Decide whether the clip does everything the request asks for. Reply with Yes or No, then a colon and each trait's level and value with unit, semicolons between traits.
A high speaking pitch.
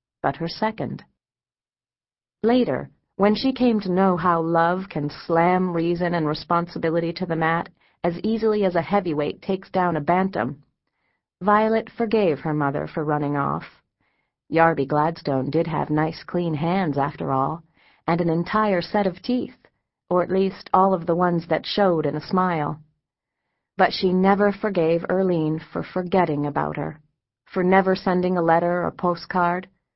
No: medium, 175 Hz